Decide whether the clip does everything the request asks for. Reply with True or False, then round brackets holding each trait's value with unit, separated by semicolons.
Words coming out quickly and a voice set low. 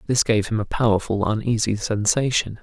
False (160 wpm; 110 Hz)